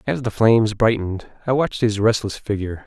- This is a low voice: Yes, low, 110 Hz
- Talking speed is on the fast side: No, average, 190 wpm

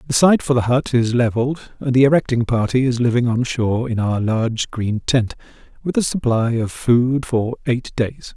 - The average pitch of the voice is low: Yes, low, 125 Hz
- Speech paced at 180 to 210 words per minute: Yes, average, 200 wpm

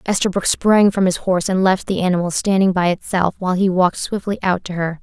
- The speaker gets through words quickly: Yes, fast, 225 wpm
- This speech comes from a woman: Yes, female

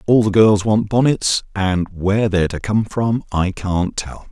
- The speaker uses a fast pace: No, average, 195 wpm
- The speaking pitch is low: Yes, low, 100 Hz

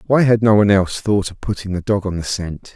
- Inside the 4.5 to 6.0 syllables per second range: No, 6.2 syllables/s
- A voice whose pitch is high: No, low, 100 Hz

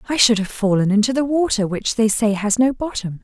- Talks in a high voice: Yes, high, 225 Hz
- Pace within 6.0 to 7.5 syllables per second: No, 5.6 syllables/s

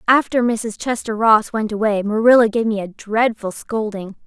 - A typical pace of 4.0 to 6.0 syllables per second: Yes, 4.7 syllables/s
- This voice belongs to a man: No, female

